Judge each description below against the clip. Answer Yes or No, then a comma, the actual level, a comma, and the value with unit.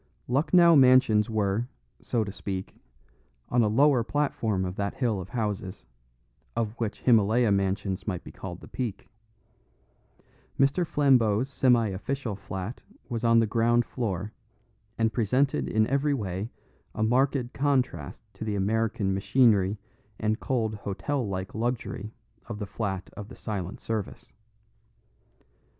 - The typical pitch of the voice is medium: No, low, 110 Hz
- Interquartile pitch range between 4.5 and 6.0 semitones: No, average, 3.8 semitones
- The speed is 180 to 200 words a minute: No, slow, 135 wpm